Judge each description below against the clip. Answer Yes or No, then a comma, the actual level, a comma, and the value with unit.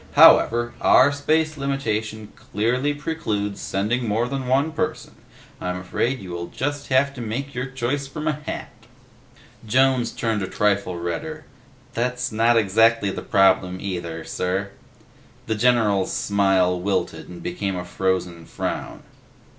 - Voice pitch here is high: No, low, 115 Hz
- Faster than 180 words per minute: No, average, 140 wpm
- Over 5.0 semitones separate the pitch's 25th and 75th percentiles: Yes, wide, 5.6 semitones